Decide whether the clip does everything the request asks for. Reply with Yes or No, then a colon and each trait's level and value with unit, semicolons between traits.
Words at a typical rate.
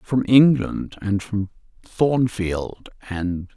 No: slow, 100 wpm